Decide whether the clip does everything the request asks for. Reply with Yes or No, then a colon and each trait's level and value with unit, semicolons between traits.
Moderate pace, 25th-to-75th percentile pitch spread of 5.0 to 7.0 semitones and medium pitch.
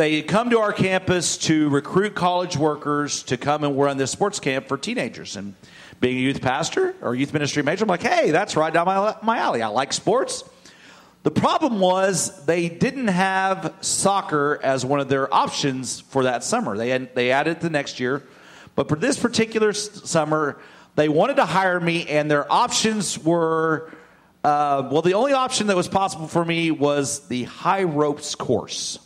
Yes: average, 185 wpm; average, 5.3 semitones; medium, 160 Hz